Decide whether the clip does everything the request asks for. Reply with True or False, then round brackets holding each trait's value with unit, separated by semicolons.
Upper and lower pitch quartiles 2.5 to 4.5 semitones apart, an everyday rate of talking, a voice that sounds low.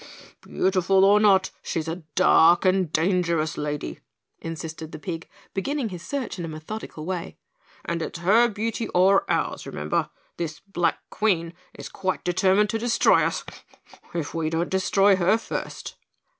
False (3.2 semitones; 150 wpm; 185 Hz)